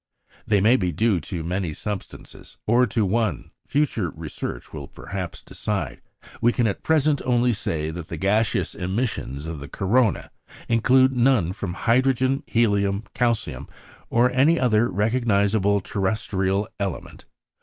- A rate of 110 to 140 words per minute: Yes, slow, 135 wpm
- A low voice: Yes, low, 105 Hz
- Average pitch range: Yes, average, 4.3 semitones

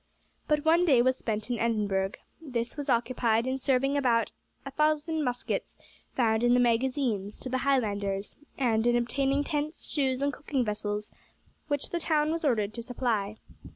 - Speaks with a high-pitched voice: Yes, very high, 250 Hz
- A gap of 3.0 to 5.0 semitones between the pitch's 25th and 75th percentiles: Yes, average, 4.1 semitones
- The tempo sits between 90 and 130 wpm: No, average, 170 wpm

